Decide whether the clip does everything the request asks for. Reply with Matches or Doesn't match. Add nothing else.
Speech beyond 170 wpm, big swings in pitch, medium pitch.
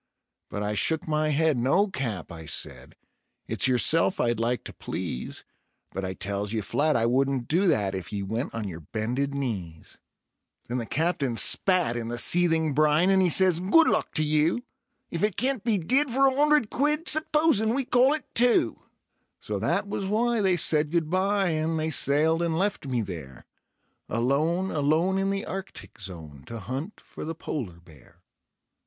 Matches